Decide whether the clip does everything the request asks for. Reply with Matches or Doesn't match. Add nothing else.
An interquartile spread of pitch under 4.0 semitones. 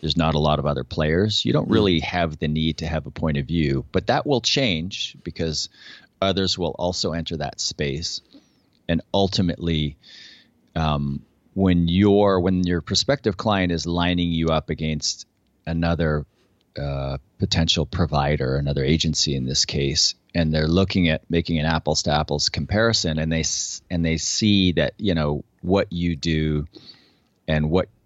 Matches